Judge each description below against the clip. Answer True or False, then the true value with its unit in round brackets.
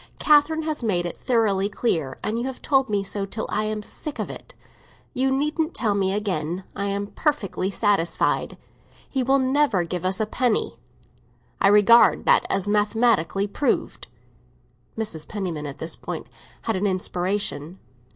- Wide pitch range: False (4.8 semitones)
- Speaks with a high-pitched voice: True (205 Hz)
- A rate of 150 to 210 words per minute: True (160 wpm)